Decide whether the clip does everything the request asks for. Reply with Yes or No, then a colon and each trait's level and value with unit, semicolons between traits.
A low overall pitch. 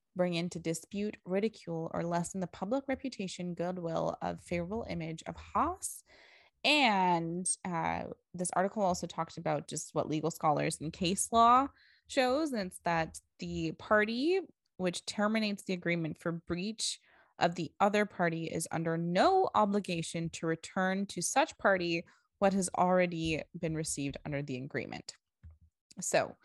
No: medium, 180 Hz